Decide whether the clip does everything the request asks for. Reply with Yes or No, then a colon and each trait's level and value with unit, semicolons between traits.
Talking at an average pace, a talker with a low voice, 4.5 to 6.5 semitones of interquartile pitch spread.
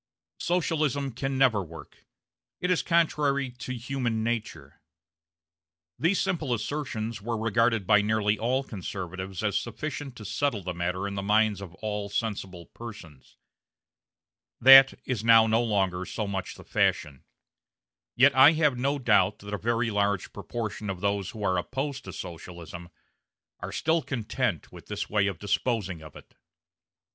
Yes: average, 150 wpm; low, 110 Hz; average, 5.1 semitones